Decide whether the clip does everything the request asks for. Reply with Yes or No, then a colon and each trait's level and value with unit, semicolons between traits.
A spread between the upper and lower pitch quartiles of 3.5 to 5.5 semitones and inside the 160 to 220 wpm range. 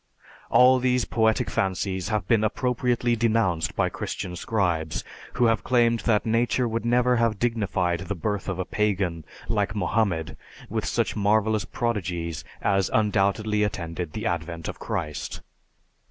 No: average, 4.1 semitones; average, 140 wpm